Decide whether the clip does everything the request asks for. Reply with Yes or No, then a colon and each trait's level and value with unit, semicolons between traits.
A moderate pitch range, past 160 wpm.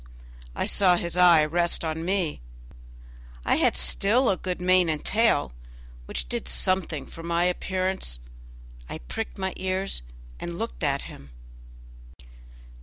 No: average, 3.6 semitones; slow, 135 wpm